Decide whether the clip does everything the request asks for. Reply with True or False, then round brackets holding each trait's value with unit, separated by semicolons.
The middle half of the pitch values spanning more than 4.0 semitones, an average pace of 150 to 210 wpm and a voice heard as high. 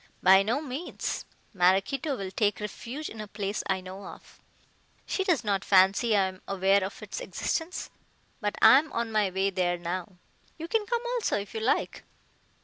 True (5.0 semitones; 180 wpm; 205 Hz)